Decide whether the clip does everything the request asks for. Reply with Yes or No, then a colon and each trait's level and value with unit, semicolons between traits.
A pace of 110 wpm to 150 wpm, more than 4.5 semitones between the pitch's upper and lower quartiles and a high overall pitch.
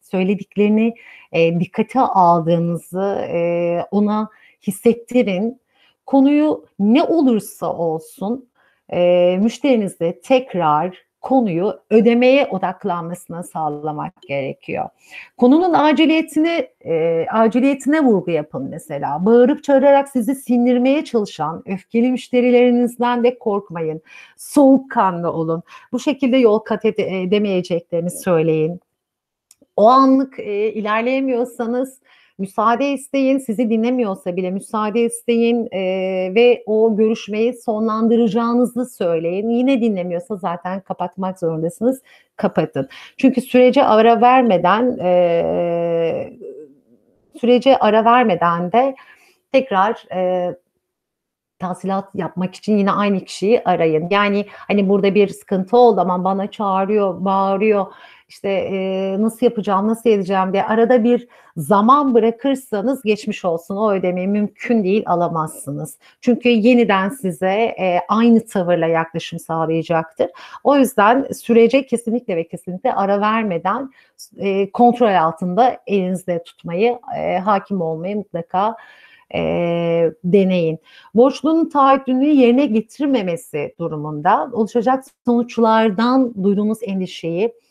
No: average, 100 wpm; average, 5.2 semitones; high, 210 Hz